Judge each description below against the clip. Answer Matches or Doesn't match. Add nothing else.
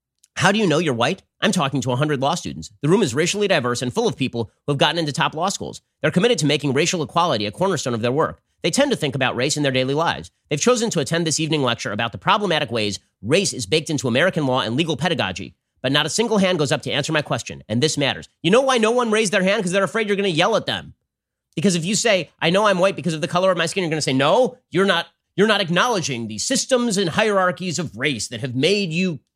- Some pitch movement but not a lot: Doesn't match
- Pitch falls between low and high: Matches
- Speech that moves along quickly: Matches